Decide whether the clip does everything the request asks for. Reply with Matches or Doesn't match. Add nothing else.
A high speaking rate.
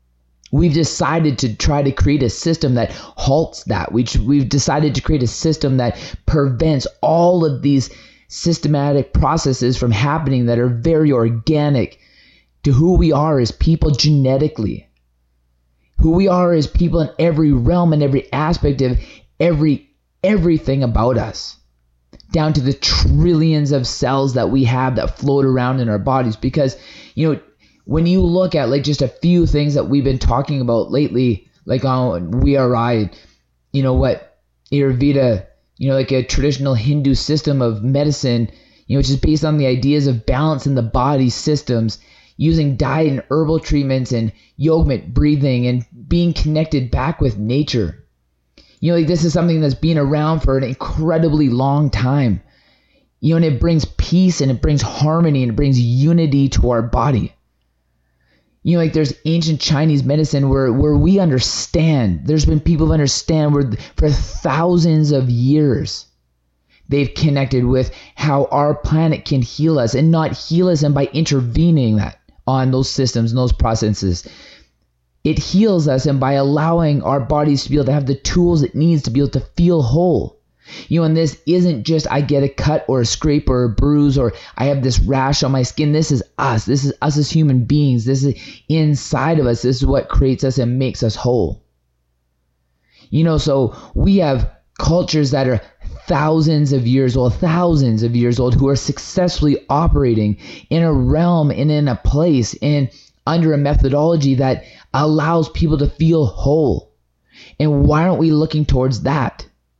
Doesn't match